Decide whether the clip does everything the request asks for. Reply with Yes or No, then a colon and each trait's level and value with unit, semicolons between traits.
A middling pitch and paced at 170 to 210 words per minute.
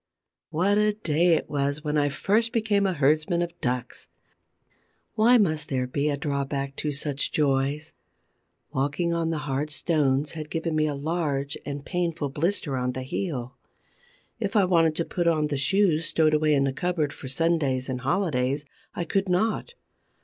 Yes: medium, 150 Hz; average, 175 wpm